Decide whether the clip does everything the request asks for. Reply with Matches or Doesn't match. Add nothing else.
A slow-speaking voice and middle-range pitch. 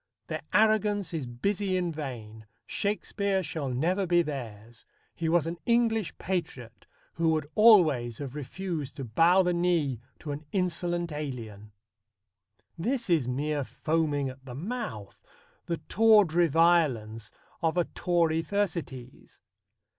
Matches